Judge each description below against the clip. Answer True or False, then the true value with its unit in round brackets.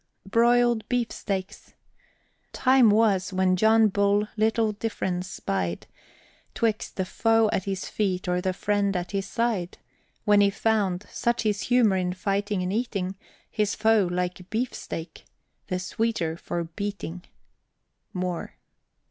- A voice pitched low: False (200 Hz)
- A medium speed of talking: False (130 wpm)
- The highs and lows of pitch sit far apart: False (3.3 semitones)